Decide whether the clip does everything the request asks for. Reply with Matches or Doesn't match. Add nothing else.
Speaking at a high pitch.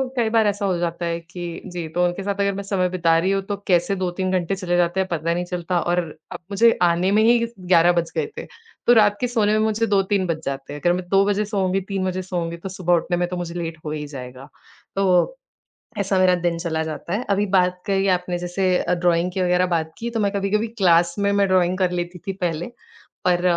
Doesn't match